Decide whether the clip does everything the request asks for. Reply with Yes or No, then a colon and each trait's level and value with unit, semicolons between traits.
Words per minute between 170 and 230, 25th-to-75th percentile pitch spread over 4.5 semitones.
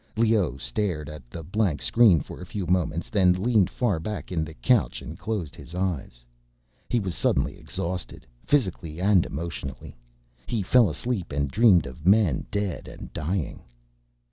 No: average, 160 wpm; average, 5.2 semitones